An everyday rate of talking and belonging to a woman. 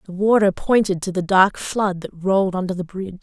No: fast, 225 wpm; female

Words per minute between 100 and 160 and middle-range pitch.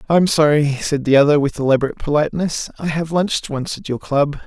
No: average, 200 wpm; medium, 150 Hz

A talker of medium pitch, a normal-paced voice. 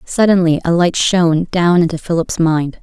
Yes: medium, 170 Hz; average, 170 wpm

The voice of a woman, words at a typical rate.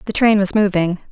No: female; fast, 215 wpm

